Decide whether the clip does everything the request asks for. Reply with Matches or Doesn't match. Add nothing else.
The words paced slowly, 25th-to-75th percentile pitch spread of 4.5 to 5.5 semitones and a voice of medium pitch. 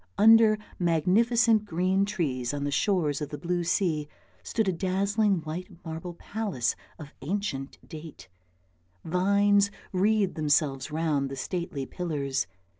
Matches